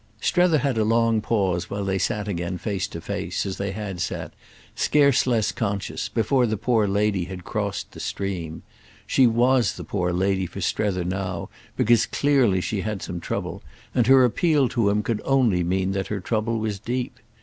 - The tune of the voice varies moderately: Yes, average, 3.7 semitones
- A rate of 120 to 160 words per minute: No, average, 185 wpm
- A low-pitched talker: Yes, low, 105 Hz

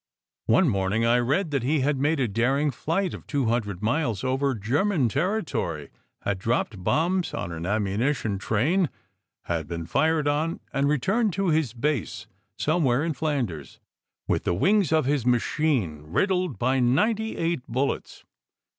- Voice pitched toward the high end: No, low, 135 Hz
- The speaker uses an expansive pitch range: Yes, wide, 6.3 semitones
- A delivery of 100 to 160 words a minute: Yes, average, 155 wpm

